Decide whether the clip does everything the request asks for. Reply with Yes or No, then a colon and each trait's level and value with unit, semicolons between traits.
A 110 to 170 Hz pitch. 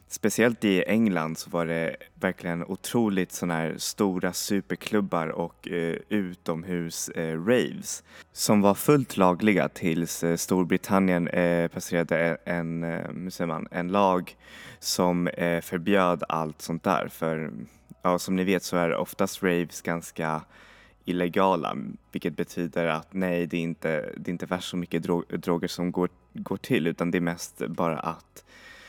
No: very low, 90 Hz